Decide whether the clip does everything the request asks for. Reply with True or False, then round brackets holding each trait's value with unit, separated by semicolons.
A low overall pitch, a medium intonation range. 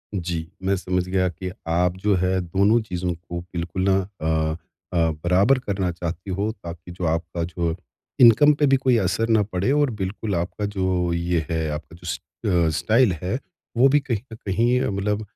True (95 Hz; 3.8 semitones)